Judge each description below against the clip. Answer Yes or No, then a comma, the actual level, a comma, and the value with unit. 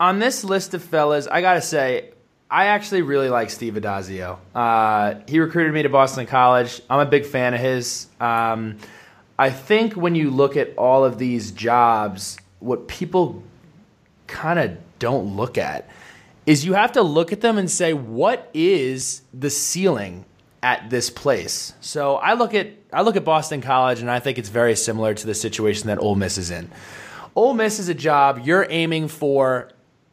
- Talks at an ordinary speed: Yes, average, 185 wpm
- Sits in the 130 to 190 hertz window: Yes, low, 135 Hz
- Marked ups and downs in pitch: Yes, wide, 6.6 semitones